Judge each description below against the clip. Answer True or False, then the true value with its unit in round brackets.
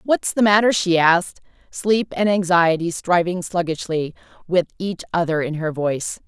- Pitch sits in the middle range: True (175 Hz)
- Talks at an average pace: True (155 wpm)